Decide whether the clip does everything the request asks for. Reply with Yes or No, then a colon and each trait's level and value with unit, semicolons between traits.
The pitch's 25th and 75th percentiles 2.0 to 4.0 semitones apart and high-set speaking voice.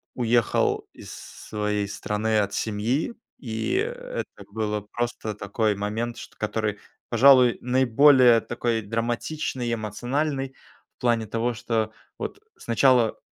No: average, 3.0 semitones; low, 115 Hz